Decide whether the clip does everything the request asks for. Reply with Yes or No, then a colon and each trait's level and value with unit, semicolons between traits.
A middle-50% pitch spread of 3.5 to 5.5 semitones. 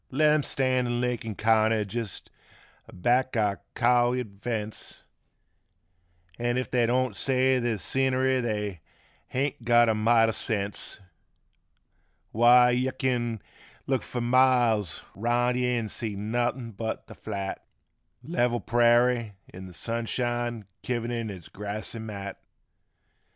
No: narrow, 2.4 semitones